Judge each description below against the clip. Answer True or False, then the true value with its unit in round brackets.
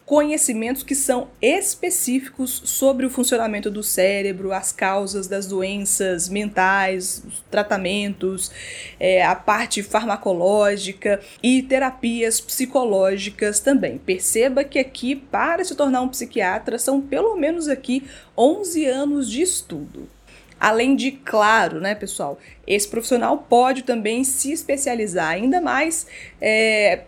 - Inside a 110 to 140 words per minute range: True (120 wpm)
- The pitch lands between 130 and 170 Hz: False (235 Hz)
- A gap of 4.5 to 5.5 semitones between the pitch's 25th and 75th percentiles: True (5.0 semitones)